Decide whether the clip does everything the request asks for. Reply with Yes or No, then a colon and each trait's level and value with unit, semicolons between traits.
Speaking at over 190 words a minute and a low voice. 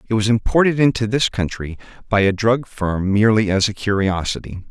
No: average, 180 wpm; low, 105 Hz